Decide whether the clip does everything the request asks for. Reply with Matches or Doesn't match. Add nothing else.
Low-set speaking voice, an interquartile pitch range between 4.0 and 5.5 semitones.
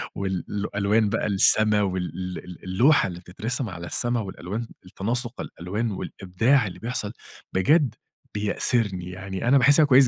Matches